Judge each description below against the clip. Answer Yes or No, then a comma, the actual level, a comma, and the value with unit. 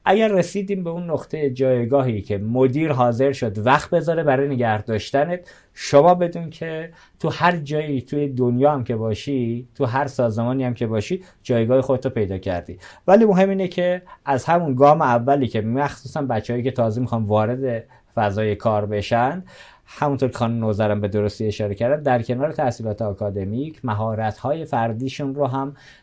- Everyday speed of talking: No, fast, 165 wpm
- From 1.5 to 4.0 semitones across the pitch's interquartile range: No, average, 4.6 semitones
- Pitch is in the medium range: No, low, 130 Hz